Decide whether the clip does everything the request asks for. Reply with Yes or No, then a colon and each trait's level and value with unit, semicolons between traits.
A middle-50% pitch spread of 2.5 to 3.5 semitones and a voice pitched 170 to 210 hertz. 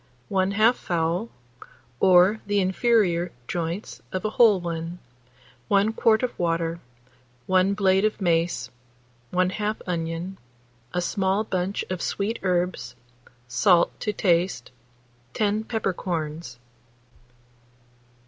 Yes: average, 3.2 semitones; medium, 185 Hz